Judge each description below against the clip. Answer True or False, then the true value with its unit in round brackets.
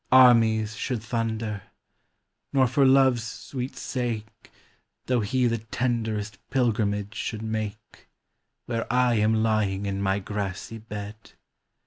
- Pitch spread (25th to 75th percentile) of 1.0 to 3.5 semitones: True (2.6 semitones)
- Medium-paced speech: False (115 wpm)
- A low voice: True (110 Hz)